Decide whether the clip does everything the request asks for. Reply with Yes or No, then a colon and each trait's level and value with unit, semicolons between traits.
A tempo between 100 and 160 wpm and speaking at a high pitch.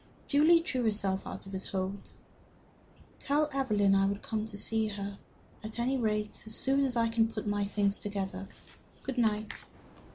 No: average, 170 wpm; high, 215 Hz